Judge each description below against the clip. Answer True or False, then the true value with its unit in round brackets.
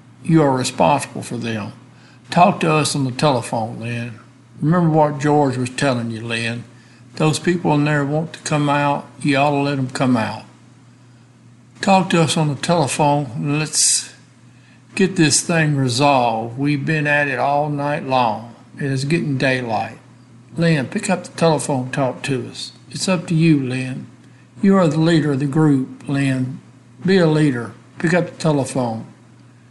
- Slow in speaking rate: False (170 wpm)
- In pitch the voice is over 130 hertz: True (140 Hz)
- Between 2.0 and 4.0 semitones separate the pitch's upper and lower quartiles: True (3.7 semitones)